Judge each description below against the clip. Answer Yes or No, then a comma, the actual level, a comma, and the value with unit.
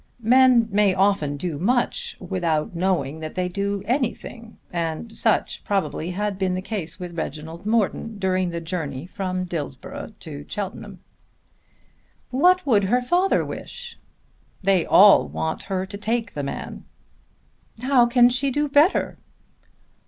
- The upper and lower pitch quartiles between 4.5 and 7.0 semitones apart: Yes, wide, 5.5 semitones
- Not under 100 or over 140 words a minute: Yes, slow, 135 wpm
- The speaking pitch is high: Yes, high, 195 Hz